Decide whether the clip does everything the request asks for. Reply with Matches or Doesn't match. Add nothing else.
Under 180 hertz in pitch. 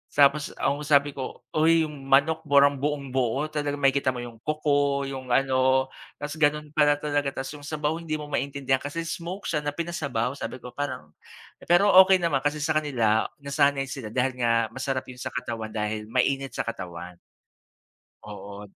Matches